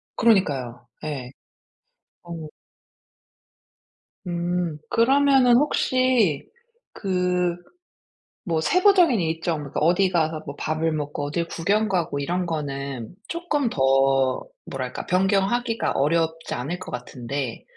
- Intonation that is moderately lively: No, wide, 5.7 semitones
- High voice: No, medium, 165 Hz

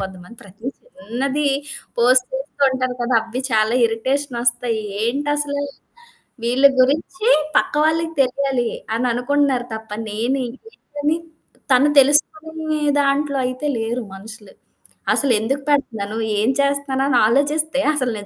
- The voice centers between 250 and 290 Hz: Yes, very high, 260 Hz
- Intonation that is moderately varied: Yes, average, 3.5 semitones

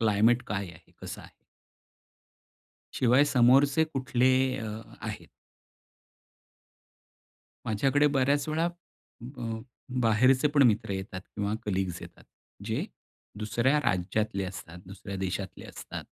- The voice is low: Yes, low, 115 Hz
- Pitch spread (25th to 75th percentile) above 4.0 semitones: Yes, wide, 5.4 semitones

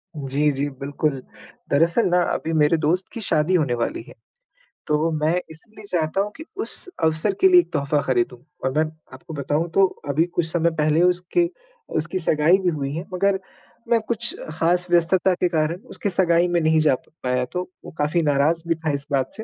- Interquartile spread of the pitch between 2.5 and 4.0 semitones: Yes, average, 3.3 semitones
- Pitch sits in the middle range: Yes, medium, 160 Hz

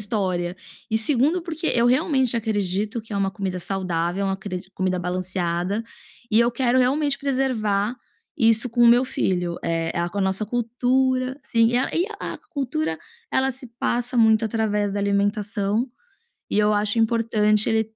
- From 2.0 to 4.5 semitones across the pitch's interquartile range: Yes, average, 4.1 semitones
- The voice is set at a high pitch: Yes, high, 215 Hz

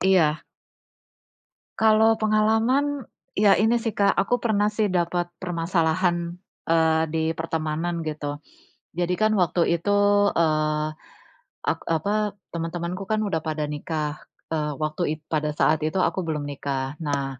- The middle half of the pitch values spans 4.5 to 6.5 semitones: Yes, average, 4.8 semitones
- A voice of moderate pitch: Yes, medium, 170 Hz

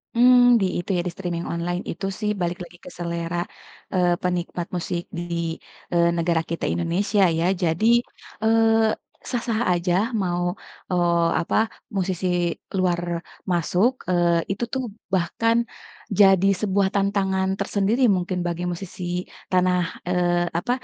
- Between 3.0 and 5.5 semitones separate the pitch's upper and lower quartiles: No, narrow, 2.4 semitones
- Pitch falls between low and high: Yes, medium, 180 Hz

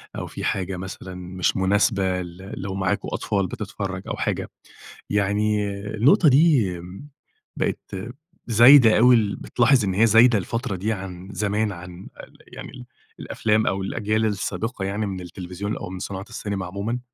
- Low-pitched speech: Yes, low, 100 Hz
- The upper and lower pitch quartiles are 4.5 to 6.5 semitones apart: No, average, 2.7 semitones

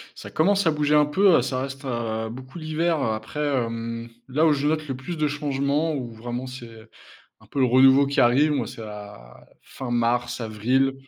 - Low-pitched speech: Yes, low, 130 Hz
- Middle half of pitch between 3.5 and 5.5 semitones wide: Yes, average, 4.1 semitones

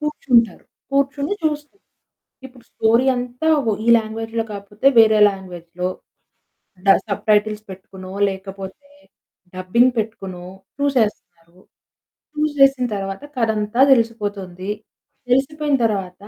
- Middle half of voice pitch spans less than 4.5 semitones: No, average, 5.3 semitones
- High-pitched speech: Yes, high, 220 Hz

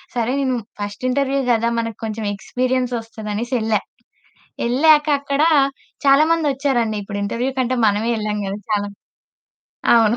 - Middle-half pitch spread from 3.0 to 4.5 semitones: Yes, average, 3.7 semitones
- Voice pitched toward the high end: Yes, high, 235 Hz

